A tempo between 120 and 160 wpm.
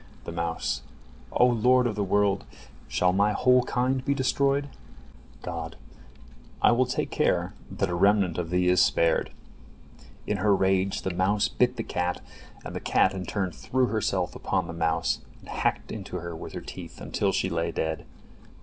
No: average, 175 wpm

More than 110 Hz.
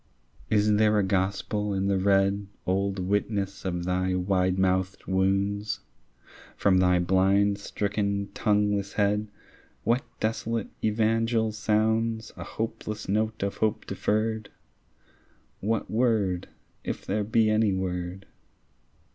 No: low, 100 Hz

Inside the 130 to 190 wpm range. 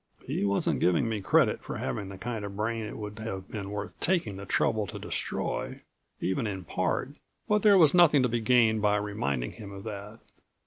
No: fast, 205 wpm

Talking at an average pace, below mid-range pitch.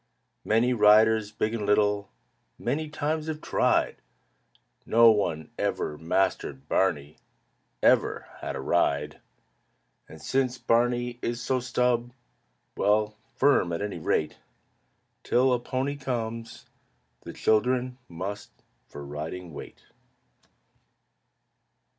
No: slow, 105 wpm; low, 110 Hz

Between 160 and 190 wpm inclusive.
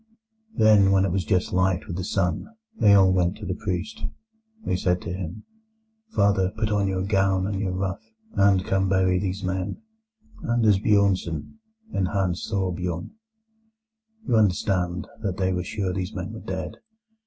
Yes: average, 165 wpm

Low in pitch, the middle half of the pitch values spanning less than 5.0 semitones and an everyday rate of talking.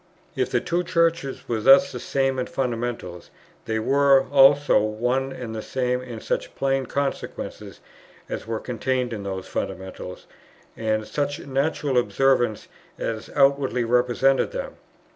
Yes: low, 130 Hz; average, 3.4 semitones; average, 145 wpm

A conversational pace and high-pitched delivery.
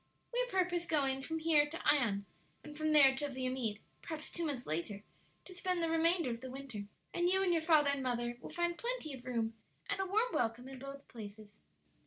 No: fast, 210 wpm; very high, 285 Hz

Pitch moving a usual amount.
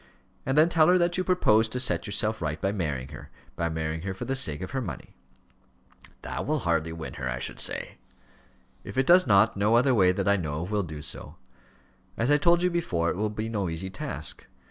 No: wide, 8.1 semitones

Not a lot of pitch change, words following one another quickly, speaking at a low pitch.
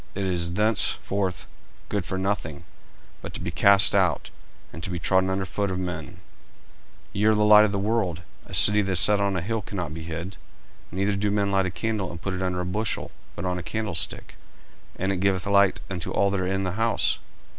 Yes: narrow, 2.1 semitones; fast, 225 wpm; very low, 95 Hz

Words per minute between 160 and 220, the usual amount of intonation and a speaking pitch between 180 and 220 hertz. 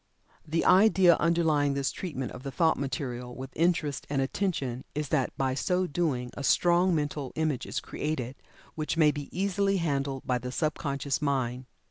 No: average, 170 wpm; average, 4.1 semitones; medium, 145 Hz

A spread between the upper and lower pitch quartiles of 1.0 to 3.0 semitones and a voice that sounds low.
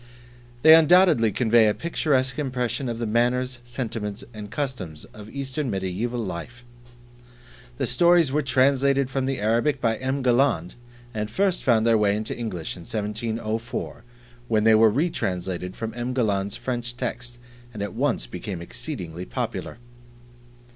No: average, 3.7 semitones; low, 120 Hz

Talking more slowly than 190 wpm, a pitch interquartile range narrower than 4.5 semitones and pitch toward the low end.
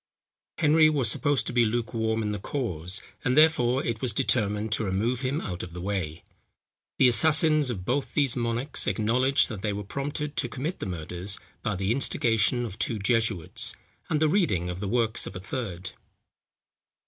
No: average, 180 wpm; average, 5.1 semitones; low, 115 Hz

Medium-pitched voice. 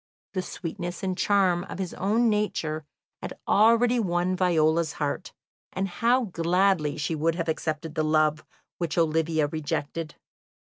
Yes: medium, 170 Hz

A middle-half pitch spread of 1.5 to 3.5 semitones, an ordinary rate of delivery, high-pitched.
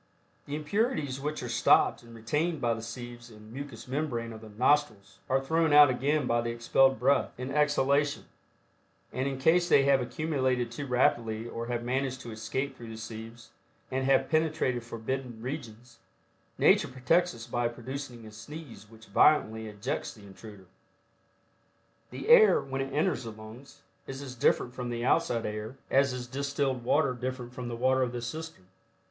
No: average, 3.2 semitones; average, 175 wpm; low, 125 Hz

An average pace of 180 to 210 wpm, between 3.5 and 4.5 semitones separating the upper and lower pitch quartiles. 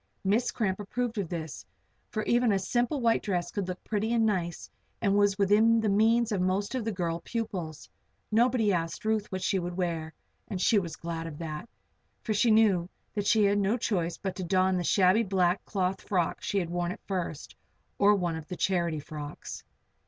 Yes: average, 200 wpm; average, 3.8 semitones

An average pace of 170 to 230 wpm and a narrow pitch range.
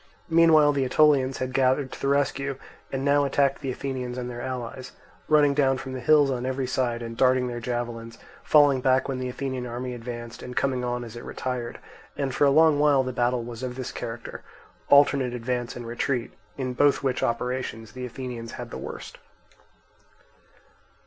Yes: average, 185 wpm; narrow, 2.1 semitones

